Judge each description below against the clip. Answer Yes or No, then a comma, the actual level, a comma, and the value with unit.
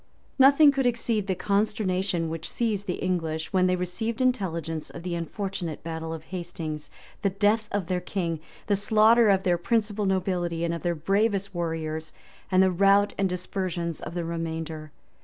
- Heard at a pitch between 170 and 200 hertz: Yes, medium, 185 Hz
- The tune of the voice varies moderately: Yes, average, 3.5 semitones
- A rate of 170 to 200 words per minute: Yes, average, 175 wpm